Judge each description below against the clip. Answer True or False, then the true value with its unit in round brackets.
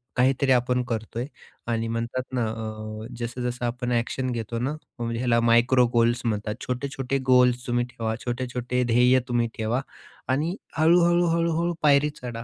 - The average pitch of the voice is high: False (125 Hz)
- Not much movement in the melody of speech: True (1.8 semitones)